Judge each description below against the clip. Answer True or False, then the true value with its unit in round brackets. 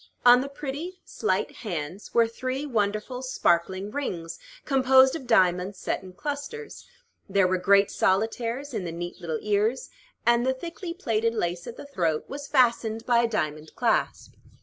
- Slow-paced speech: False (160 wpm)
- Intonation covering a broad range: True (6.0 semitones)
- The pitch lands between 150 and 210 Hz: False (230 Hz)